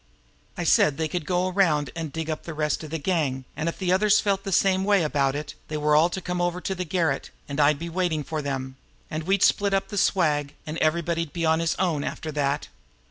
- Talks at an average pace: No, fast, 245 wpm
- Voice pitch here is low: No, medium, 160 Hz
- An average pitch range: Yes, average, 3.3 semitones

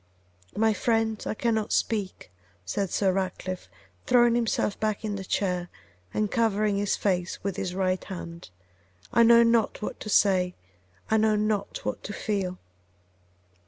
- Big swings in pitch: No, average, 2.8 semitones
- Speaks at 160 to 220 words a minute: No, average, 150 wpm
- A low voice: No, high, 205 Hz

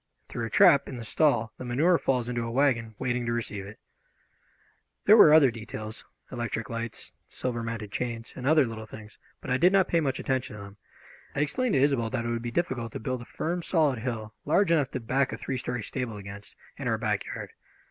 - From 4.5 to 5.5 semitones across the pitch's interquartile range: No, average, 3.5 semitones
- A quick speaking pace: Yes, fast, 220 wpm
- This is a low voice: Yes, low, 120 Hz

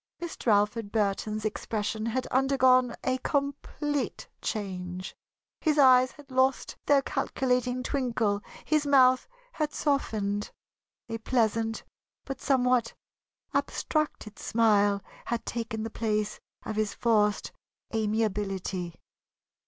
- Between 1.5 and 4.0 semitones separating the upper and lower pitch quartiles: Yes, average, 3.7 semitones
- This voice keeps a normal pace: No, slow, 105 wpm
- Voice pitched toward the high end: Yes, high, 230 Hz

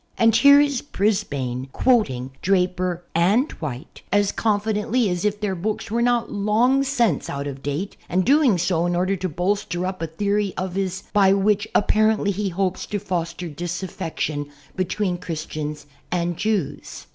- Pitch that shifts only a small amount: No, average, 3.6 semitones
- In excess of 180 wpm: No, average, 160 wpm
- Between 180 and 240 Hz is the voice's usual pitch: Yes, high, 190 Hz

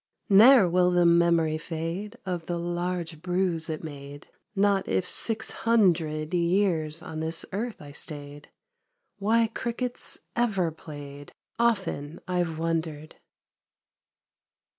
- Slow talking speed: Yes, slow, 115 wpm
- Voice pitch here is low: No, medium, 170 Hz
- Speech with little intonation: No, average, 3.7 semitones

